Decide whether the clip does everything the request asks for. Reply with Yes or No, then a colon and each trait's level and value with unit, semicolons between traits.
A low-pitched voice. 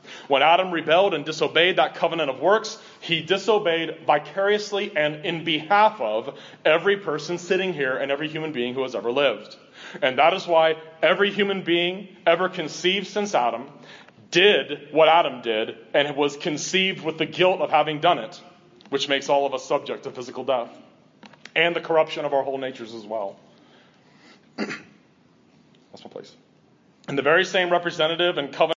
No: medium, 165 Hz